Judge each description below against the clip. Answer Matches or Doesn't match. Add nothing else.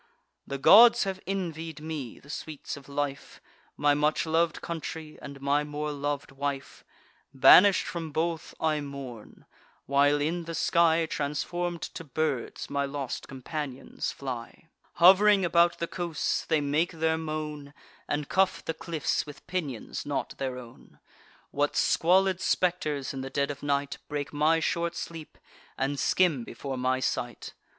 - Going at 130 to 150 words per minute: Matches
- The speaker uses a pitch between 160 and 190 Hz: Doesn't match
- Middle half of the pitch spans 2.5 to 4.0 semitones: Matches